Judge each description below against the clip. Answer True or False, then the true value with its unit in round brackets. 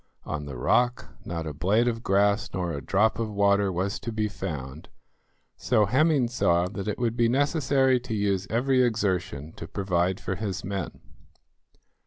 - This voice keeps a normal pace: True (170 wpm)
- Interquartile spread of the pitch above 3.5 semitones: True (4.7 semitones)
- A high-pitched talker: False (100 Hz)